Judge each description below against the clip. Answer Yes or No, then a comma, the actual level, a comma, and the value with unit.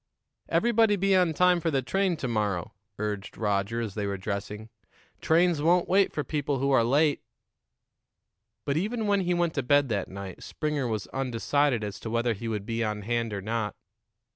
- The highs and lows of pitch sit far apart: Yes, wide, 7.5 semitones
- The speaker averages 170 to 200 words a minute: Yes, average, 190 wpm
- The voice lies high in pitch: No, low, 125 Hz